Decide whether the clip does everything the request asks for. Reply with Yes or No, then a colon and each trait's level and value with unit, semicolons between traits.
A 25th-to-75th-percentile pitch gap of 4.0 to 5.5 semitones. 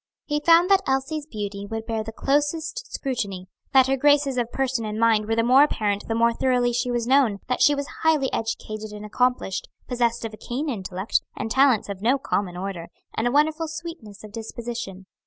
Yes: average, 4.5 semitones